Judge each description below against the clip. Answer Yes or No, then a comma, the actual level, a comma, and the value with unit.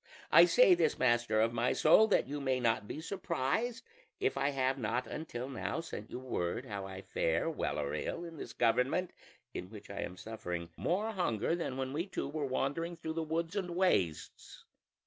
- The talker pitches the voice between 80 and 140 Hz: Yes, low, 135 Hz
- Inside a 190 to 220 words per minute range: Yes, average, 200 wpm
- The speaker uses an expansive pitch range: Yes, wide, 6.8 semitones